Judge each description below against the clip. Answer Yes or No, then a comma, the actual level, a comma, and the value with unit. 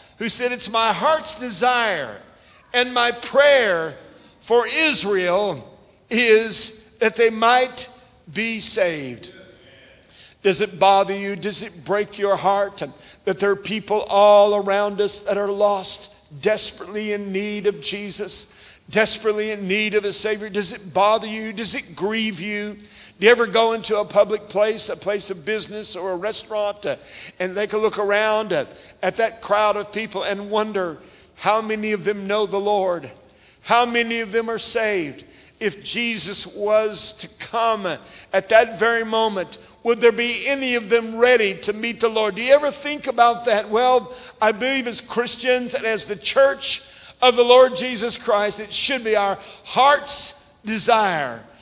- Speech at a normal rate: Yes, average, 165 wpm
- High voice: Yes, high, 215 Hz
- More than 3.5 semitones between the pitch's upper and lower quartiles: No, narrow, 2.5 semitones